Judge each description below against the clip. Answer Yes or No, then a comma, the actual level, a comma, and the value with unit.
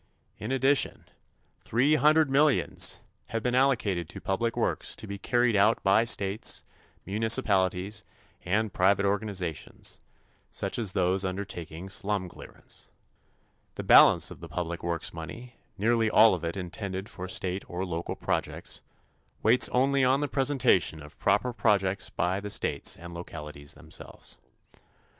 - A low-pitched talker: Yes, low, 100 Hz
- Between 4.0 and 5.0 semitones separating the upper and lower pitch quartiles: Yes, average, 4.5 semitones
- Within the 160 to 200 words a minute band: No, average, 140 wpm